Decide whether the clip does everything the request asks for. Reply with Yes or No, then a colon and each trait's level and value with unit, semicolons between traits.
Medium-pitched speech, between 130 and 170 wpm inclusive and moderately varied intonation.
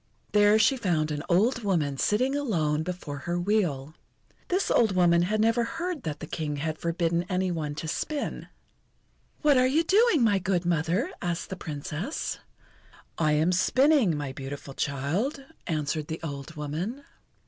No: medium, 175 Hz; average, 160 wpm; wide, 6.7 semitones